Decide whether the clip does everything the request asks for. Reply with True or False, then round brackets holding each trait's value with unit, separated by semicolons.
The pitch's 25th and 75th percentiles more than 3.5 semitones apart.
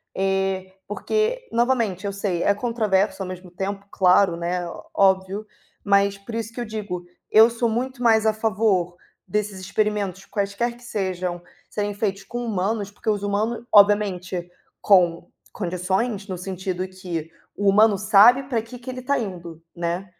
False (2.9 semitones)